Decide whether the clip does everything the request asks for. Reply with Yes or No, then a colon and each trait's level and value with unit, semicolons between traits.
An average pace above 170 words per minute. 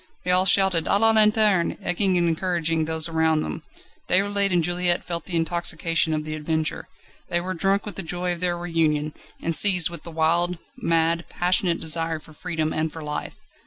Yes: average, 190 wpm